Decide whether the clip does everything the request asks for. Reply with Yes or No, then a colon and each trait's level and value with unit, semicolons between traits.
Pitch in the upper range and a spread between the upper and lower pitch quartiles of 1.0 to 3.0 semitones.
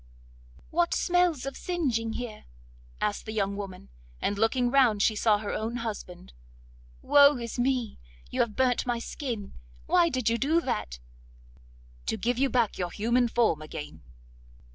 No: high, 235 Hz; average, 3.8 semitones